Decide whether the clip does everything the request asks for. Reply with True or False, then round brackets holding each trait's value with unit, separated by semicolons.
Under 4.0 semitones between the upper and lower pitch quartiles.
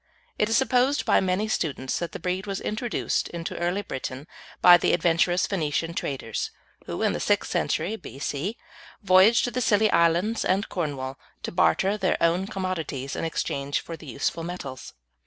False (4.4 semitones)